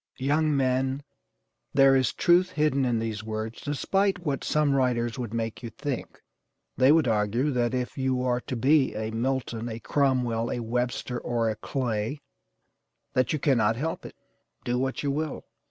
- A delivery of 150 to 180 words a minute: Yes, average, 170 wpm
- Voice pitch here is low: Yes, low, 130 Hz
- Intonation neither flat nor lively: Yes, average, 3.3 semitones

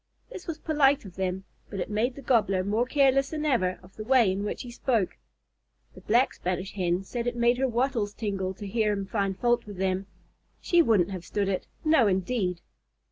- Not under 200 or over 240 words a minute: Yes, fast, 205 wpm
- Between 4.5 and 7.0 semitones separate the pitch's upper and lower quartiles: Yes, average, 4.8 semitones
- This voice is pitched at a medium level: No, high, 210 Hz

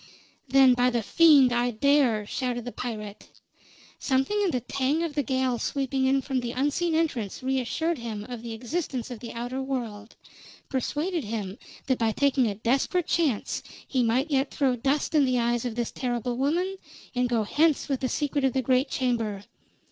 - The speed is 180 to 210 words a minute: Yes, average, 185 wpm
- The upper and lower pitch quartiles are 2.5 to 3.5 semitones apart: Yes, average, 2.9 semitones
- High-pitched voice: Yes, very high, 255 Hz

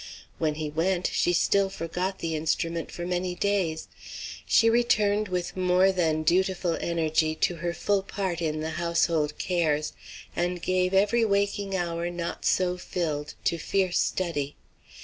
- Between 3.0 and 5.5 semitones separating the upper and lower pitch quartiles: No, narrow, 2.6 semitones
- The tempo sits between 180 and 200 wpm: No, average, 150 wpm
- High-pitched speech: No, medium, 175 Hz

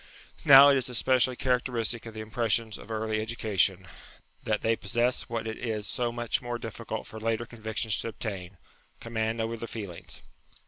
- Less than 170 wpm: No, average, 180 wpm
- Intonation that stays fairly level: Yes, narrow, 1.6 semitones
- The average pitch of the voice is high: No, low, 115 Hz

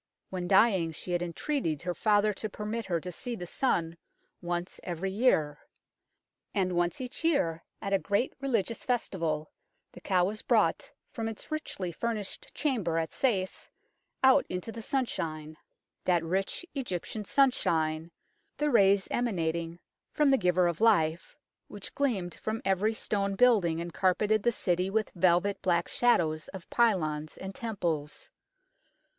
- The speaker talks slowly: No, average, 145 wpm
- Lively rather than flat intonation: No, average, 4.8 semitones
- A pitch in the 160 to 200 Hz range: Yes, high, 190 Hz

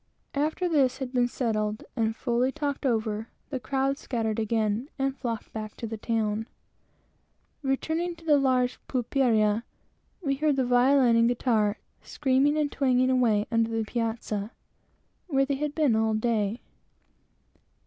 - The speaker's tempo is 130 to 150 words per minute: Yes, average, 145 wpm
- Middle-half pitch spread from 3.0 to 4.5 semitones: Yes, average, 3.5 semitones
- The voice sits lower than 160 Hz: No, high, 245 Hz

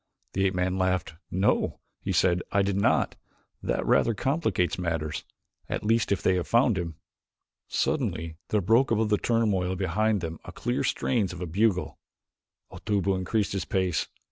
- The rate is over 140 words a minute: Yes, average, 165 wpm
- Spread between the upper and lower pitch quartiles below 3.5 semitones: Yes, average, 3.1 semitones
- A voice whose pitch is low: Yes, very low, 95 Hz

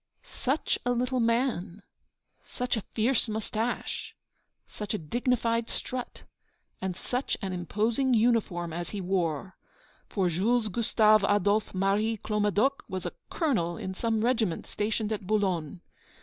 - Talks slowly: Yes, slow, 130 wpm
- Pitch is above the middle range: Yes, high, 215 Hz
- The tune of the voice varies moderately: Yes, average, 4.0 semitones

